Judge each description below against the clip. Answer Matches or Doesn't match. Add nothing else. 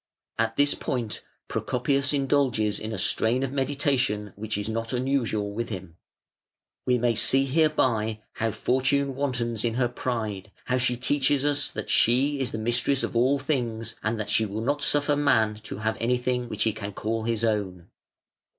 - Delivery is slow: Doesn't match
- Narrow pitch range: Doesn't match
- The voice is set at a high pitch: Doesn't match